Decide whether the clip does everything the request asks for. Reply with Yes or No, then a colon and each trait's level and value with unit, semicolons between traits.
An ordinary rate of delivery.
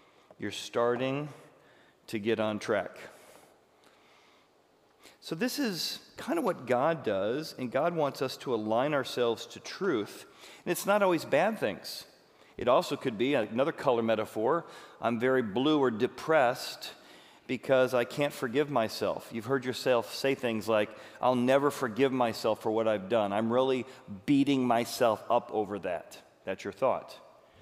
Yes: average, 150 wpm